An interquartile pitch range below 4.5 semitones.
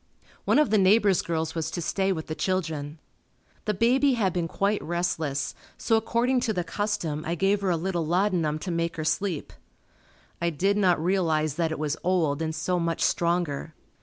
Yes: average, 3.7 semitones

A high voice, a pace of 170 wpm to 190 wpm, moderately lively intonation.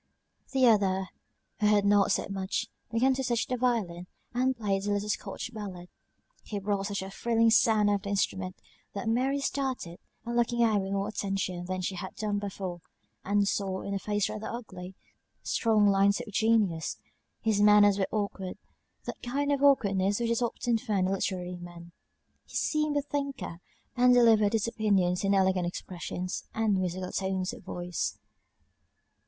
Yes: high, 205 Hz; average, 175 wpm; average, 3.3 semitones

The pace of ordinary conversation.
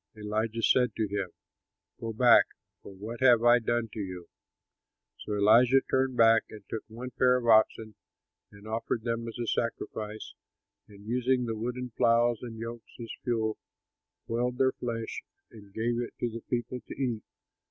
Yes: average, 165 wpm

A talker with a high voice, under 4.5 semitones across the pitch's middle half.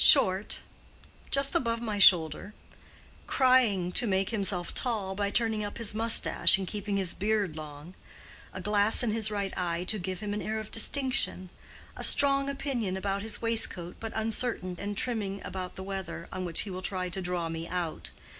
Yes: high, 200 Hz; average, 3.3 semitones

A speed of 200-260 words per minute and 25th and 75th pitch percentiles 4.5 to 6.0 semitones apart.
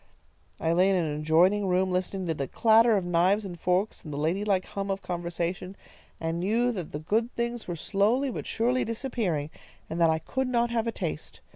Yes: fast, 205 wpm; average, 4.9 semitones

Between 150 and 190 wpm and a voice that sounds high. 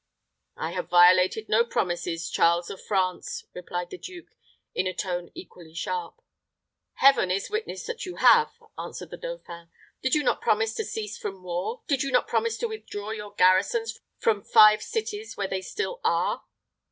Yes: average, 170 wpm; high, 210 Hz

